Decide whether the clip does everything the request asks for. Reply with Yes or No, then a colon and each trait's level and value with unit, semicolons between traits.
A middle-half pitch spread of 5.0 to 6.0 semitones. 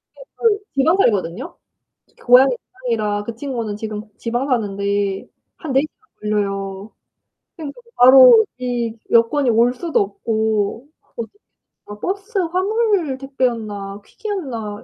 Yes: average, 5.3 semitones